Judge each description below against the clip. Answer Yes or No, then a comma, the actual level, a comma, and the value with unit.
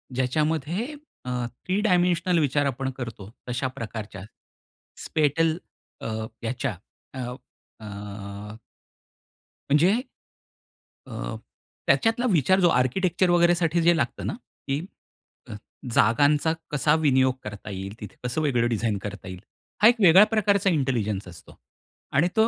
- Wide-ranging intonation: Yes, wide, 7.7 semitones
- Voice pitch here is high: No, medium, 140 Hz